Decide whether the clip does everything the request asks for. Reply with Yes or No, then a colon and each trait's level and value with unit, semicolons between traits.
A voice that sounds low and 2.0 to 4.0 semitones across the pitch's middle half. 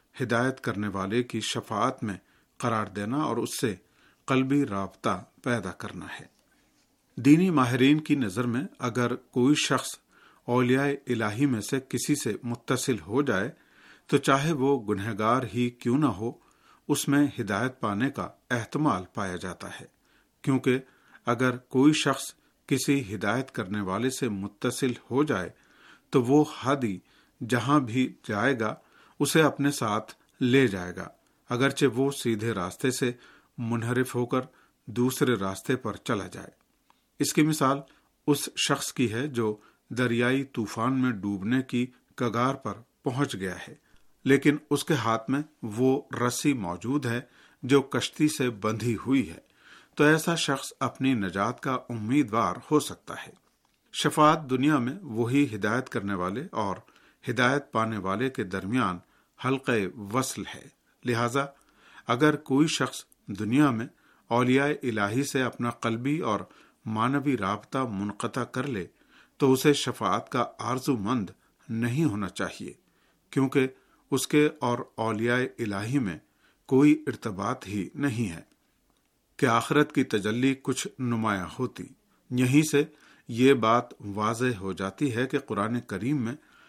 Yes: low, 125 Hz; average, 3.6 semitones